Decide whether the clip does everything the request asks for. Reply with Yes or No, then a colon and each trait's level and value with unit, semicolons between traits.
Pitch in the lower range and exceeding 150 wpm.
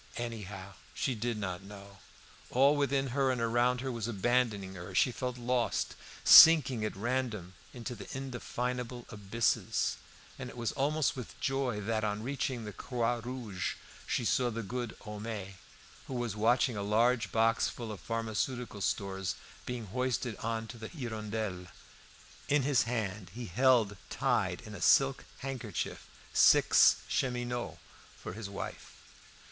No: low, 115 Hz; average, 145 wpm